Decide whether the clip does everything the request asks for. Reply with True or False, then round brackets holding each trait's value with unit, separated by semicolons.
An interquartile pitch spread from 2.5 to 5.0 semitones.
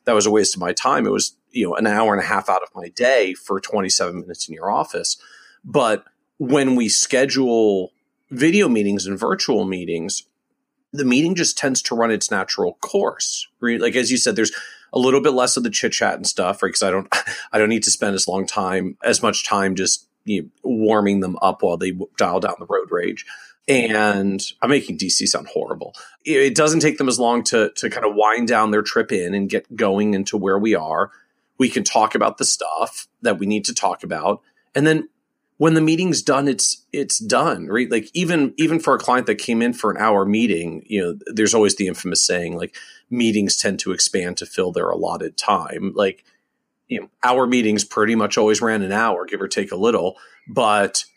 False (5.4 semitones)